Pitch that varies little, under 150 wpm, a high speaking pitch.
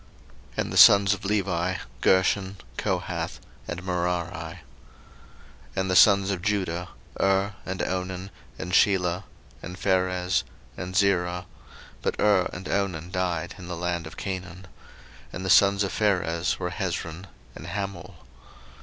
No: narrow, 1.7 semitones; average, 140 wpm; very low, 90 Hz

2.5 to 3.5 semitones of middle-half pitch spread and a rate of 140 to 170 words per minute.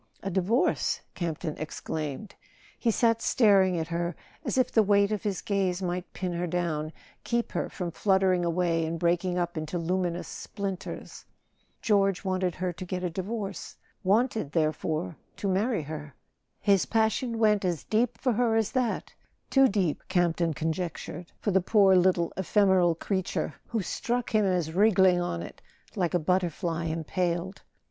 Yes: average, 3.0 semitones; average, 160 wpm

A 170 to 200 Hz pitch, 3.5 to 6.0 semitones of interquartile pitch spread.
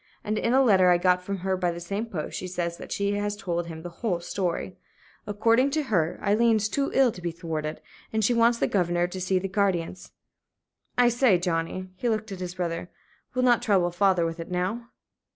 Yes: high, 190 Hz; average, 3.9 semitones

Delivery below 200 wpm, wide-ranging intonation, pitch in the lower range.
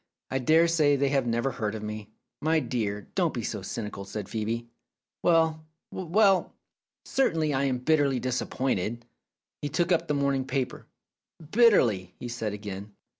Yes: average, 160 wpm; wide, 6.4 semitones; low, 130 Hz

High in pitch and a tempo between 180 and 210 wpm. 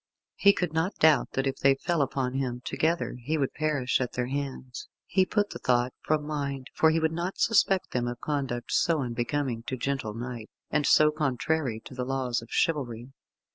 No: low, 135 Hz; average, 195 wpm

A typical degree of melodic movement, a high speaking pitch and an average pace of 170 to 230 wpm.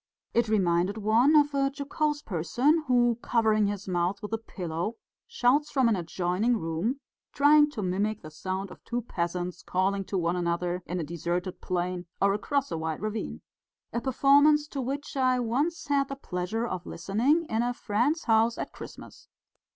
No: wide, 6.9 semitones; high, 220 Hz; average, 175 wpm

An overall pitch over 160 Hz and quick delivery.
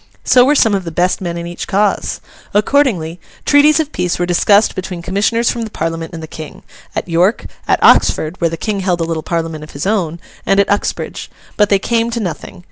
Yes: medium, 185 Hz; fast, 215 wpm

